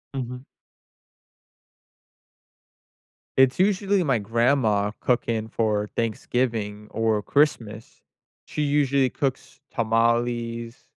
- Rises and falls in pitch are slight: No, average, 3.2 semitones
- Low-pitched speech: Yes, low, 120 Hz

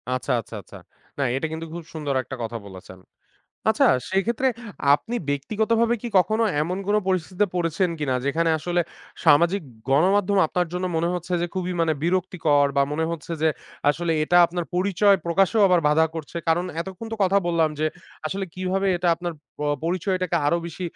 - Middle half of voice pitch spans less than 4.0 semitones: Yes, average, 2.9 semitones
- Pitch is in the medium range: Yes, medium, 175 Hz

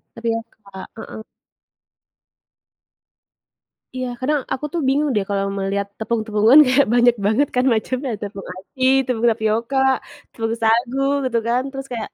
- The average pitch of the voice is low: No, high, 230 Hz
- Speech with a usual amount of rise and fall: Yes, average, 3.0 semitones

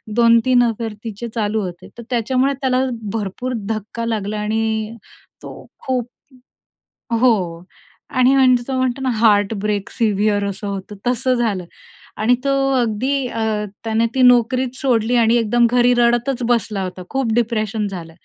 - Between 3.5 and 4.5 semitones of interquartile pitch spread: No, average, 2.9 semitones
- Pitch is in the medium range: No, high, 230 Hz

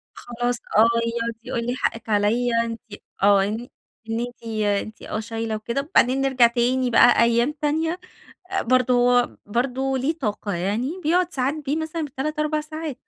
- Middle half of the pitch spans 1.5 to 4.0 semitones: Yes, average, 3.3 semitones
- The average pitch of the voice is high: Yes, high, 245 Hz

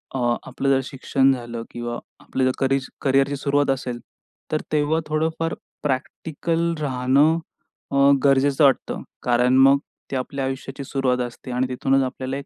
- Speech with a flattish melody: Yes, narrow, 1.9 semitones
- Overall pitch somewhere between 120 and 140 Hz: Yes, low, 135 Hz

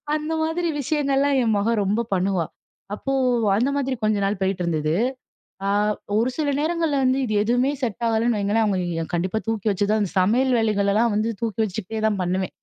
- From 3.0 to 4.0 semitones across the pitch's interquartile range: No, average, 4.6 semitones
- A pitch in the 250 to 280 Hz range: No, high, 220 Hz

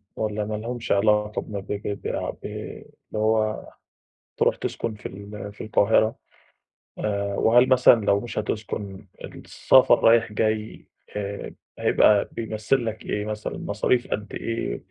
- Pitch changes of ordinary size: No, narrow, 1.5 semitones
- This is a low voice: Yes, low, 105 Hz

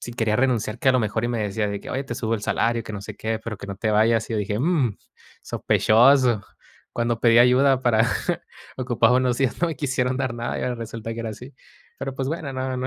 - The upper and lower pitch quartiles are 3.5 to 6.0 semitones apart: No, average, 2.7 semitones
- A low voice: Yes, low, 120 Hz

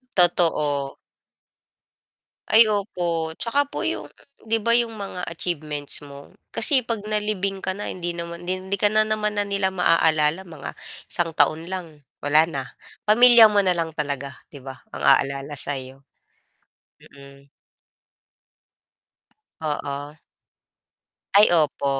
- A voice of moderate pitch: Yes, medium, 170 Hz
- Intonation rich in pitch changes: Yes, wide, 5.8 semitones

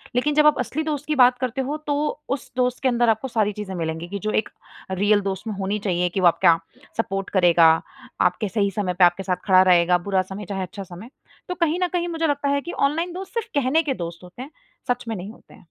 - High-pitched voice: Yes, high, 215 Hz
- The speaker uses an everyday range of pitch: No, wide, 7.4 semitones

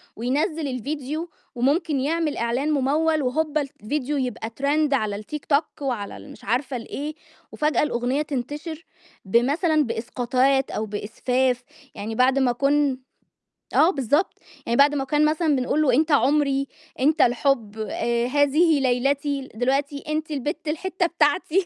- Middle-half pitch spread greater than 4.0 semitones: No, average, 3.4 semitones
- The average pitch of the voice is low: No, very high, 280 Hz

